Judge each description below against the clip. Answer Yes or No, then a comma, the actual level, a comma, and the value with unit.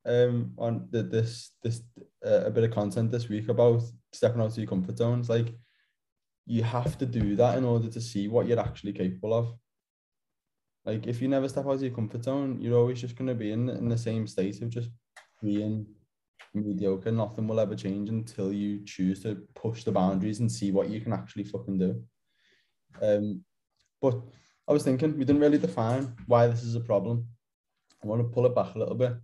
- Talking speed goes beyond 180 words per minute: Yes, fast, 205 wpm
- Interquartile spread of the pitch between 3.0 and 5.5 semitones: No, narrow, 2.5 semitones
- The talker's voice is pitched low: Yes, low, 115 Hz